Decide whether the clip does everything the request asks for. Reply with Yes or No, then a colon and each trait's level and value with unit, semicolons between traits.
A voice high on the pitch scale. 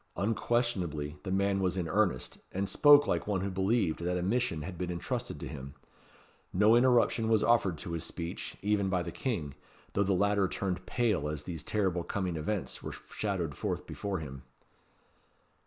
No: very low, 95 Hz